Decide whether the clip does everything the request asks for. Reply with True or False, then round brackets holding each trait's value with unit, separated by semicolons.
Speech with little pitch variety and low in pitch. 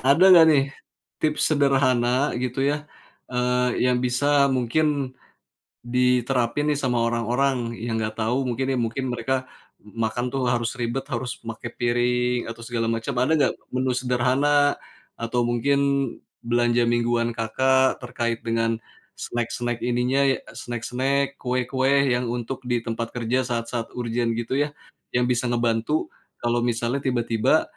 True (2.0 semitones; 125 Hz)